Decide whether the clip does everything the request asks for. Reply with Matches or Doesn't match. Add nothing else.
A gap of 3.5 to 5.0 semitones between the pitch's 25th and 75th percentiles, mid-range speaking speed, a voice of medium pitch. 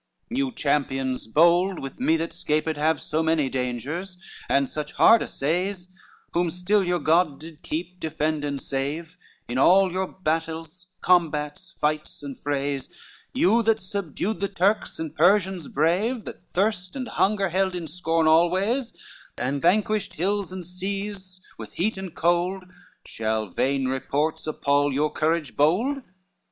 Matches